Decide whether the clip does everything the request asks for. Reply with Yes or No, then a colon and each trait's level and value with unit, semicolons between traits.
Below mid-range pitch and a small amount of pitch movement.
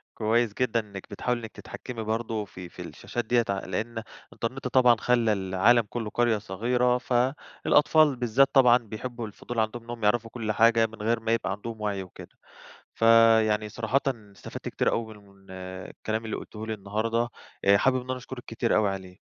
Yes: low, 115 Hz; narrow, 2.3 semitones